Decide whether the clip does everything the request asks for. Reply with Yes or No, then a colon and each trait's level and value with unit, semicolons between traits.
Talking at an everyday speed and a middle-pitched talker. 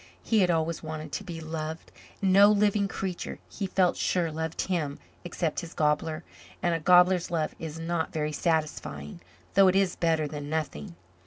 Yes: average, 175 wpm; medium, 165 Hz